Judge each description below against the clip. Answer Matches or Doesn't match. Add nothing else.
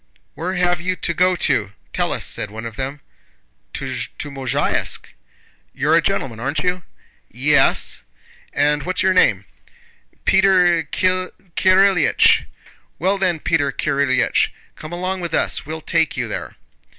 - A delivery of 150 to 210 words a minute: Doesn't match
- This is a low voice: Doesn't match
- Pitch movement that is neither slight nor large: Matches